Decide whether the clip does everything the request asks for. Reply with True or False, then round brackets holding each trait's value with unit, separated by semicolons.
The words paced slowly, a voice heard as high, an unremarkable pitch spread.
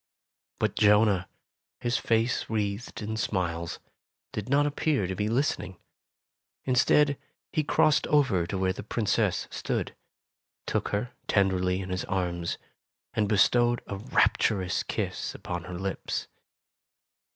False (125 wpm; 105 Hz; 4.4 semitones)